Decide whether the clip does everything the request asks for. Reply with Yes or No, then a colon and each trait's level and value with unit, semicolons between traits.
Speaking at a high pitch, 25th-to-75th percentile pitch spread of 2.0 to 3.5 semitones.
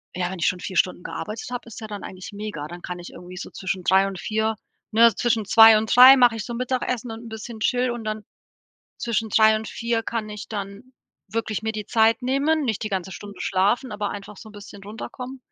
Yes: high, 220 Hz; average, 2.8 semitones